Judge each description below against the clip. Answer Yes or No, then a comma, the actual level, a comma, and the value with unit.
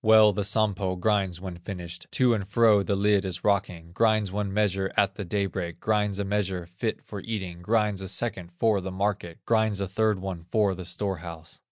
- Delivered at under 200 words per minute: No, fast, 205 wpm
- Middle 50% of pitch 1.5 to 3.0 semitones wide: Yes, narrow, 2.4 semitones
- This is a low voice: Yes, low, 100 Hz